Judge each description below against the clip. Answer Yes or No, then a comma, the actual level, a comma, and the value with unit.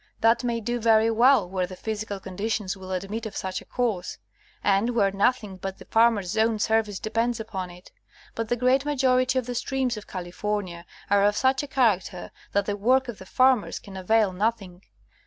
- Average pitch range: Yes, average, 3.7 semitones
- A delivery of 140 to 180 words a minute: No, average, 195 wpm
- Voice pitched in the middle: No, high, 220 Hz